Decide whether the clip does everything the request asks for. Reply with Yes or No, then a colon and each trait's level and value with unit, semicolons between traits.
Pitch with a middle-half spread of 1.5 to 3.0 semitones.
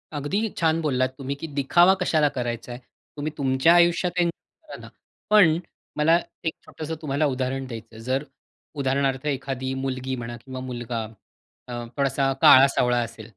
No: average, 3.4 semitones